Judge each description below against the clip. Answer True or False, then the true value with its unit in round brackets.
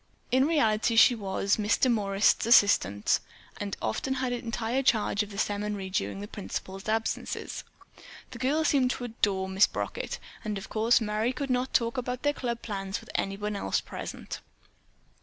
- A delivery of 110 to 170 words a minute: True (160 wpm)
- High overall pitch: True (220 Hz)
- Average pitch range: True (3.9 semitones)